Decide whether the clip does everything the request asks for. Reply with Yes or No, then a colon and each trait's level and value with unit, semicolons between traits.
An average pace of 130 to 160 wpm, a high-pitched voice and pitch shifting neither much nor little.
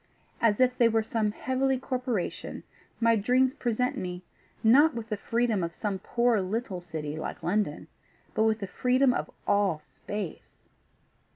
Yes: average, 155 wpm; high, 220 Hz; average, 4.3 semitones